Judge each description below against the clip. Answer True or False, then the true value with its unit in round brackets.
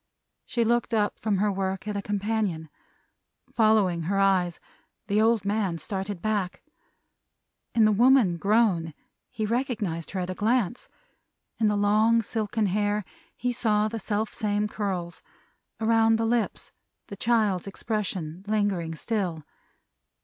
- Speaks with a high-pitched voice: True (210 Hz)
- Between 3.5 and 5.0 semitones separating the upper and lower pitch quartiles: False (2.8 semitones)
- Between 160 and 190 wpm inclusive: False (135 wpm)